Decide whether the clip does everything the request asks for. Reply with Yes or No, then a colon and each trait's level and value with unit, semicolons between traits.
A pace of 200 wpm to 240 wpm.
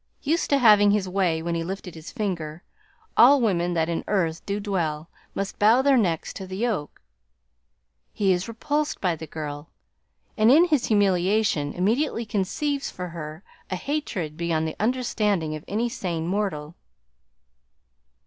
No: average, 155 wpm